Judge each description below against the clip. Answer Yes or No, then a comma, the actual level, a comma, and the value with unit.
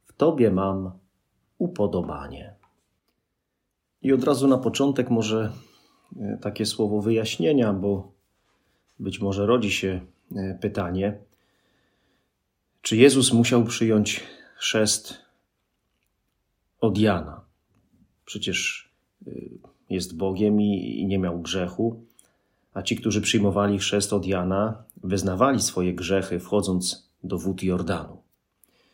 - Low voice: Yes, low, 100 Hz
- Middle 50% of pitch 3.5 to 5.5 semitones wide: No, average, 2.7 semitones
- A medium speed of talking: No, slow, 95 wpm